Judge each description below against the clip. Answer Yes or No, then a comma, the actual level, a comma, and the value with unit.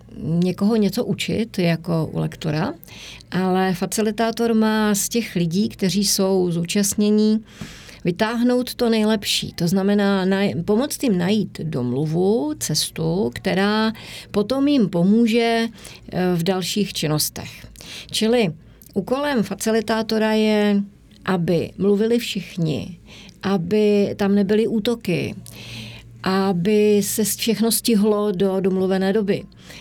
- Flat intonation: No, average, 3.0 semitones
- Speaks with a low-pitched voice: No, high, 200 Hz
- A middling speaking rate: No, slow, 100 wpm